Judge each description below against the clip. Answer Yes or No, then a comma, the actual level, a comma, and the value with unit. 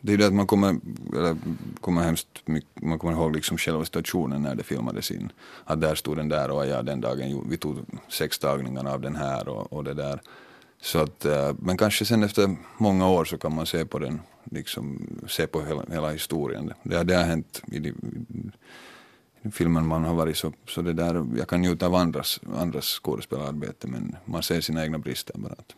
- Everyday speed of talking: No, fast, 210 wpm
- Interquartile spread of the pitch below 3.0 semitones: Yes, narrow, 2.5 semitones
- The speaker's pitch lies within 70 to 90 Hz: Yes, very low, 80 Hz